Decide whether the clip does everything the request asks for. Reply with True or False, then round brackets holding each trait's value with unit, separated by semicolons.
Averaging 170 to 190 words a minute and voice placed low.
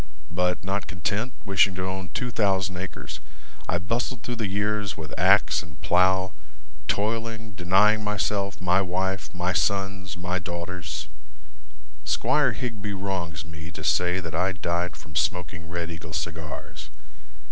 False (140 wpm; 95 Hz)